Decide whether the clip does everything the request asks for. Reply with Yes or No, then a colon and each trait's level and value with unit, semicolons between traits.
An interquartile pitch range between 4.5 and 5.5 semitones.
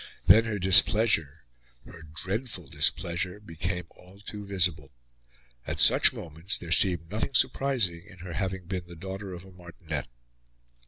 No: average, 2.9 semitones